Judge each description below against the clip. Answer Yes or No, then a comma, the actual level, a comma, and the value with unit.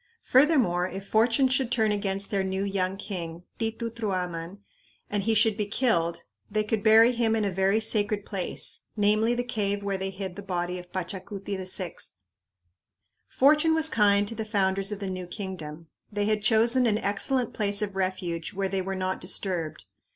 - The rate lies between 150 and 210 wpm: Yes, average, 180 wpm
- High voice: Yes, high, 200 Hz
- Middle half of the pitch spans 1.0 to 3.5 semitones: Yes, average, 2.8 semitones